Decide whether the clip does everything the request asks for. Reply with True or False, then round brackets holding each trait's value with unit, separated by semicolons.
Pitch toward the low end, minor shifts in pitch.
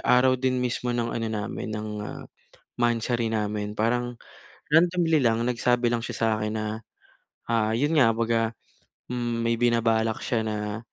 True (115 Hz; 1.8 semitones)